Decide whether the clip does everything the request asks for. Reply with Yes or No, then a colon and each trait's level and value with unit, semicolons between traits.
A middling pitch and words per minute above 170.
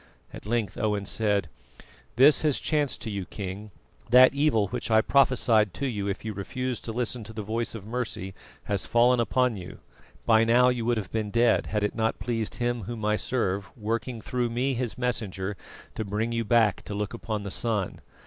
No: low, 115 Hz; average, 195 wpm